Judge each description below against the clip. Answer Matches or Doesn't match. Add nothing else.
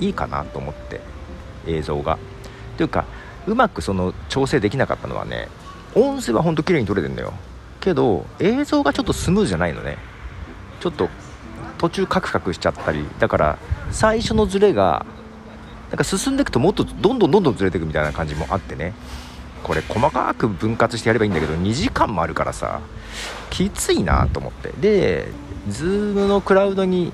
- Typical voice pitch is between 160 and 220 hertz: Doesn't match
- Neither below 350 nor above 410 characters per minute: Matches